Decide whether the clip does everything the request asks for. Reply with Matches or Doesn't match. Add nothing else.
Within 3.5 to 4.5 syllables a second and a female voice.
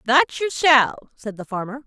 Matches